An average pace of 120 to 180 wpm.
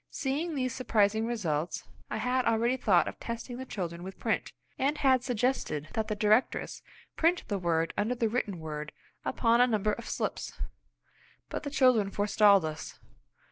Yes: average, 165 wpm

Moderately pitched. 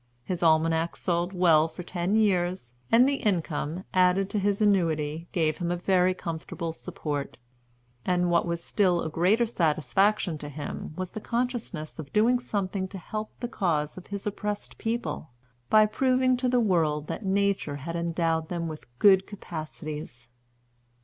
Yes: medium, 180 Hz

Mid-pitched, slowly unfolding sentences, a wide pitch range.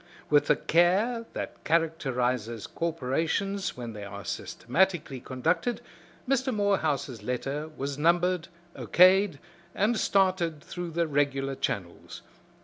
Yes: medium, 160 Hz; slow, 110 wpm; wide, 6.0 semitones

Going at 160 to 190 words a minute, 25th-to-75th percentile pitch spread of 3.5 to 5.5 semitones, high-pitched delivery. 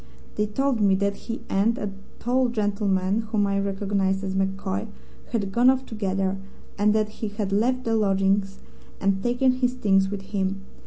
No: average, 170 wpm; average, 2.7 semitones; high, 205 Hz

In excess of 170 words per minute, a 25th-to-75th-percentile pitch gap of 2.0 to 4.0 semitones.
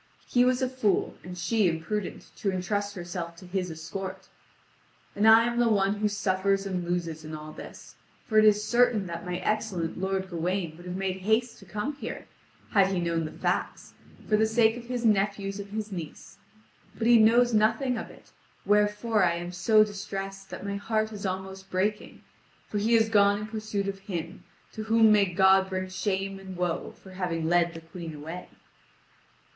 Yes: average, 190 wpm; average, 3.1 semitones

